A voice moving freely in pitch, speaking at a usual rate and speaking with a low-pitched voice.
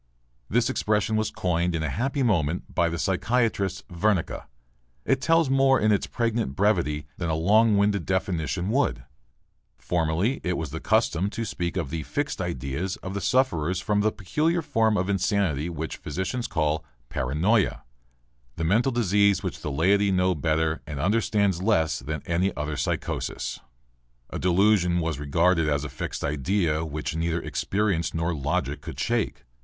No: average, 4.8 semitones; average, 160 wpm; very low, 90 Hz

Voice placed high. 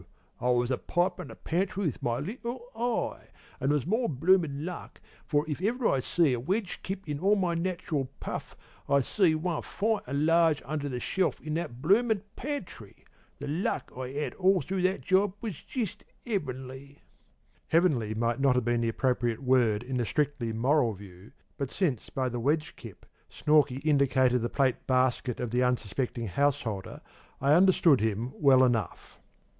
No: medium, 145 Hz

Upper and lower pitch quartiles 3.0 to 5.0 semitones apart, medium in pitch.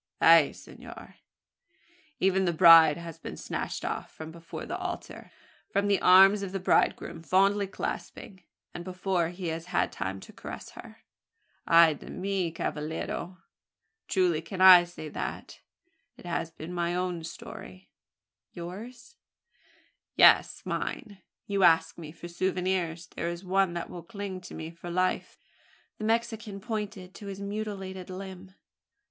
No: narrow, 2.5 semitones; medium, 180 Hz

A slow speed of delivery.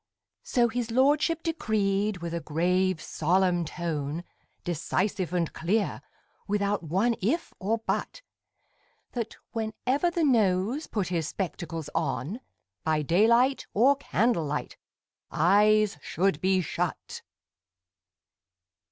Yes: slow, 105 wpm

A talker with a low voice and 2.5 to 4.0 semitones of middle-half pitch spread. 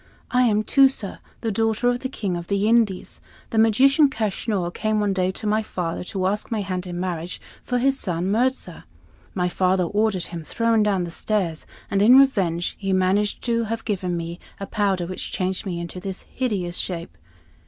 No: high, 200 Hz; average, 3.7 semitones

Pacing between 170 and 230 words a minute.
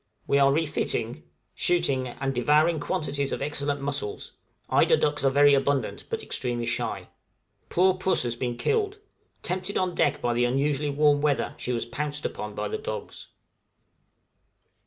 No: average, 155 wpm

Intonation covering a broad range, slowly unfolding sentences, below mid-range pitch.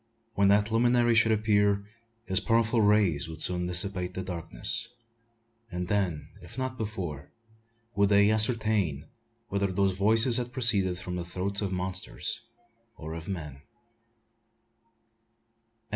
No: average, 3.5 semitones; slow, 130 wpm; low, 100 Hz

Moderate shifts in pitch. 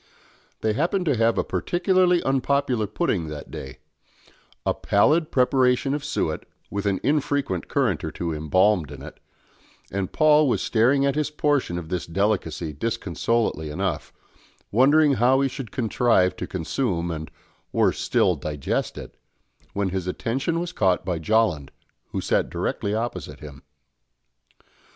No: wide, 8.0 semitones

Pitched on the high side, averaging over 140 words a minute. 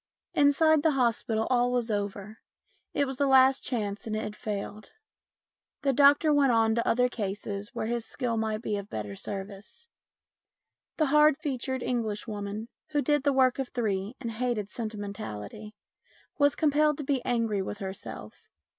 Yes: high, 235 Hz; average, 160 wpm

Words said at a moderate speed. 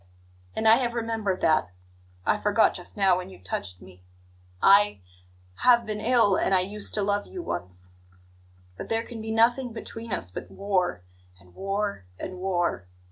Yes: average, 170 wpm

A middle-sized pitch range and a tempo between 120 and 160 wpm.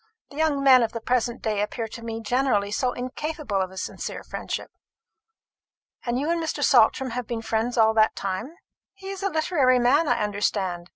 No: average, 4.2 semitones; average, 190 wpm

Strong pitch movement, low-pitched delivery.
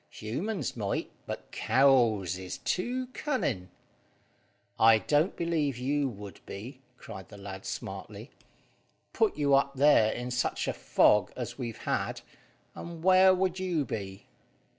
Yes: wide, 8.1 semitones; low, 130 Hz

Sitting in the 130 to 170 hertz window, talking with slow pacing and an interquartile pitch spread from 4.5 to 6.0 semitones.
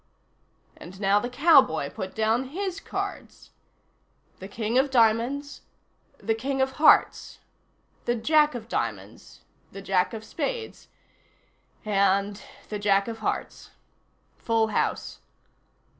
No: high, 225 Hz; slow, 115 wpm; average, 4.8 semitones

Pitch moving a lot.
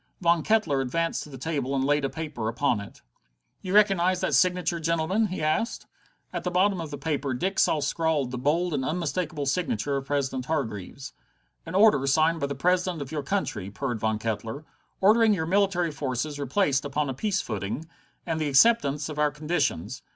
No: average, 4.6 semitones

